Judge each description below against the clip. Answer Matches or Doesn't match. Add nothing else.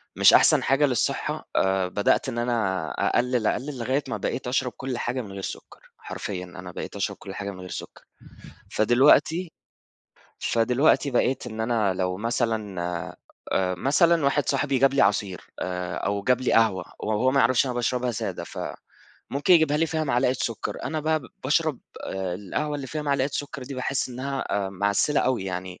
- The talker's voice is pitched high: Doesn't match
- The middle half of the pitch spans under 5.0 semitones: Doesn't match